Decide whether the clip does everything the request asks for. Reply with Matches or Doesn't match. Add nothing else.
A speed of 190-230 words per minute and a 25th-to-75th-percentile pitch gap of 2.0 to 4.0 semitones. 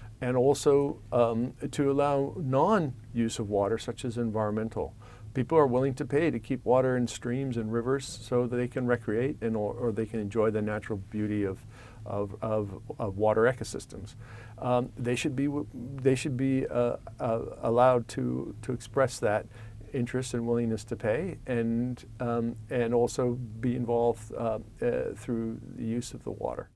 Doesn't match